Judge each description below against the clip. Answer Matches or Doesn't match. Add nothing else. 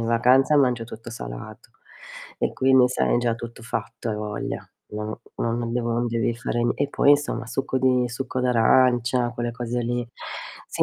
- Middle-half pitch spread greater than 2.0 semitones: Doesn't match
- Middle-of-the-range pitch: Doesn't match